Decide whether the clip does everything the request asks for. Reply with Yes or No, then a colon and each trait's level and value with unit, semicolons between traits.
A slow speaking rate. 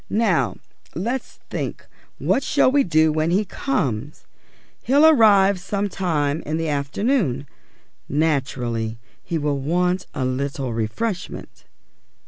Yes: slow, 115 wpm